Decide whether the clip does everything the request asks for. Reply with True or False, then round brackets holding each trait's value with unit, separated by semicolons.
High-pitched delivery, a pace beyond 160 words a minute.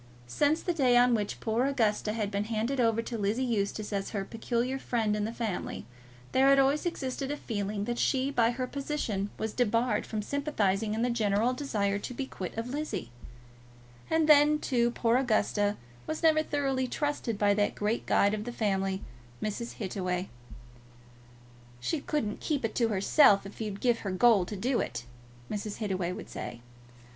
True (230 Hz; 180 wpm)